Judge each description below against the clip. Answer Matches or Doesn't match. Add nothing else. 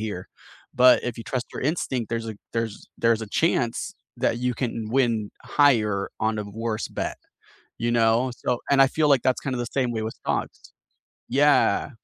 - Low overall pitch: Matches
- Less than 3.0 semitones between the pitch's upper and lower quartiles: Matches